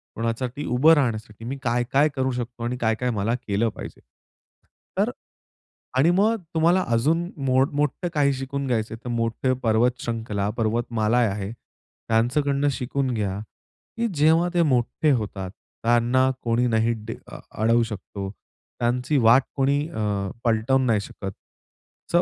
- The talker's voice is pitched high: No, low, 120 Hz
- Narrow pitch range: No, average, 3.5 semitones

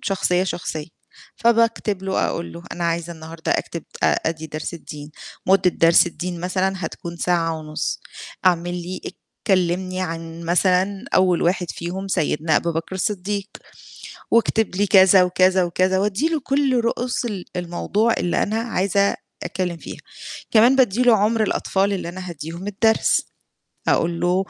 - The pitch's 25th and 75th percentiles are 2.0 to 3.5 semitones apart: Yes, average, 2.8 semitones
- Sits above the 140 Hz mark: Yes, medium, 185 Hz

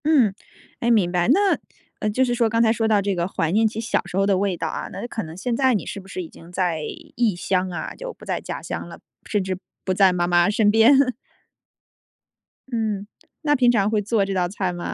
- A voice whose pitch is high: Yes, high, 205 Hz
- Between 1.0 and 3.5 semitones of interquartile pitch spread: No, average, 4.1 semitones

